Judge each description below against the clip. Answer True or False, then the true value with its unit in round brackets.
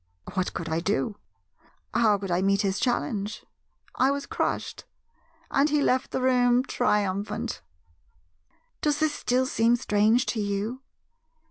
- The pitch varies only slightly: False (4.1 semitones)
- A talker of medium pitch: False (225 Hz)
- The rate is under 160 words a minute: True (135 wpm)